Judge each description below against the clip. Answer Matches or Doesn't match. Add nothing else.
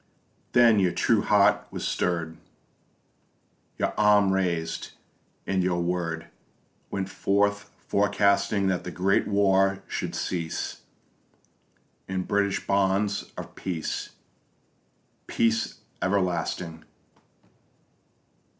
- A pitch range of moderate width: Doesn't match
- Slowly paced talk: Matches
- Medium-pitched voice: Doesn't match